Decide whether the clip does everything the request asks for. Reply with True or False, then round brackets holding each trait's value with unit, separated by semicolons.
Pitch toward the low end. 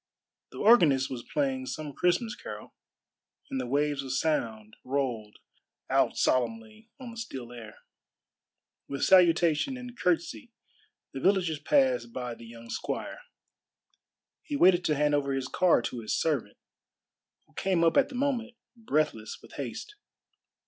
False (150 Hz)